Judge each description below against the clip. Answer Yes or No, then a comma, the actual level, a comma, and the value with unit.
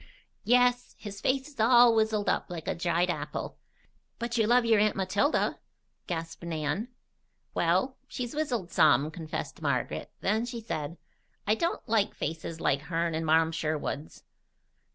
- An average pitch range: No, wide, 6.4 semitones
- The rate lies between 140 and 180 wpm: Yes, average, 150 wpm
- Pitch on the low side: No, high, 190 Hz